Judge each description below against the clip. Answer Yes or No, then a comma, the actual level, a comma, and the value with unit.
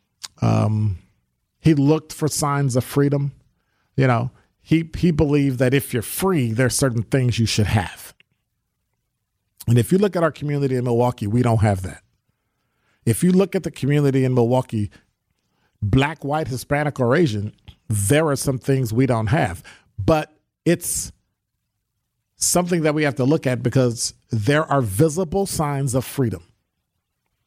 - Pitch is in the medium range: No, low, 125 Hz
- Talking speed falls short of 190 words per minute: Yes, average, 155 wpm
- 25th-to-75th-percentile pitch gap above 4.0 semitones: Yes, average, 4.8 semitones